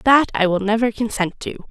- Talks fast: Yes, fast, 210 wpm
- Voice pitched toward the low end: No, high, 220 Hz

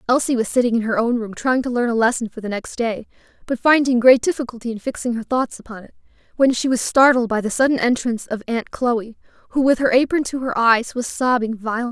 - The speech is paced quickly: Yes, fast, 235 wpm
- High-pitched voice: Yes, high, 240 Hz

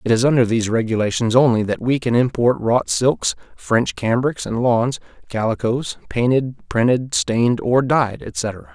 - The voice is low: Yes, low, 120 Hz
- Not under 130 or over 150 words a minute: No, average, 160 wpm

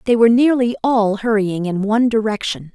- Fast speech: No, average, 175 wpm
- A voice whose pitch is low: No, high, 220 Hz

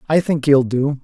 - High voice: No, medium, 140 Hz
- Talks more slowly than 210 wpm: No, fast, 235 wpm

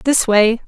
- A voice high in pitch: Yes, high, 230 Hz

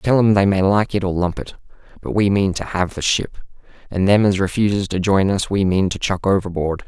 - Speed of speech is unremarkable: No, fast, 245 wpm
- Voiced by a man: Yes, male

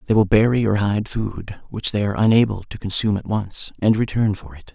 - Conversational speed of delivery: No, fast, 230 wpm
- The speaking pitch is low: Yes, low, 105 Hz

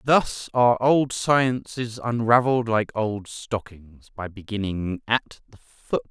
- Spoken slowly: Yes, slow, 130 wpm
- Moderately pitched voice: No, low, 115 Hz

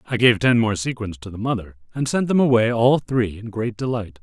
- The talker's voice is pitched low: Yes, low, 115 Hz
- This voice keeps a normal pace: No, fast, 240 wpm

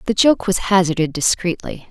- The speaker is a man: No, female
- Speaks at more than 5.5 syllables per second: No, 5.1 syllables/s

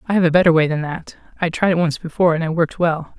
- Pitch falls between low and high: Yes, medium, 165 Hz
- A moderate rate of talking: No, fast, 300 wpm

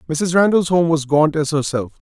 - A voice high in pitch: No, medium, 160 Hz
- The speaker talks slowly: No, average, 200 wpm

